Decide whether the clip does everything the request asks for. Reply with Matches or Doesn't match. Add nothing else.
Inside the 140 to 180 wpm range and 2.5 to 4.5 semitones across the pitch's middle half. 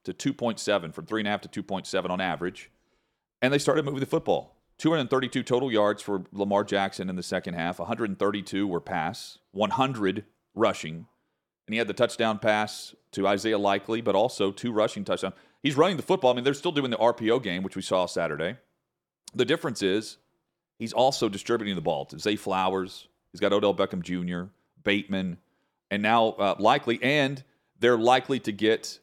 Matches